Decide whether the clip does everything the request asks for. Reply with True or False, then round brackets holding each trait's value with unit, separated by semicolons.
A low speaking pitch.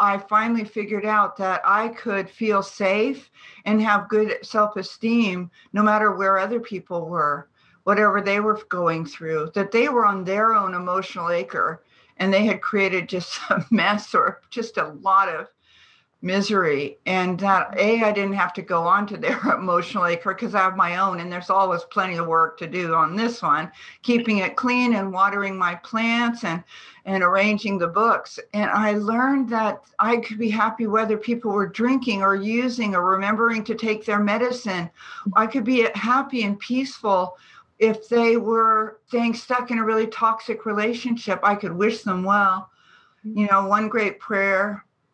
False (205 Hz)